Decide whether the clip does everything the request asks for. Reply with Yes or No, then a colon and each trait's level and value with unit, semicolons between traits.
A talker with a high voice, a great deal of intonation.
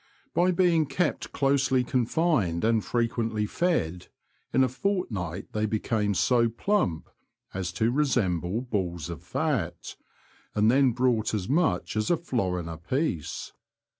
No: low, 115 Hz; wide, 6.5 semitones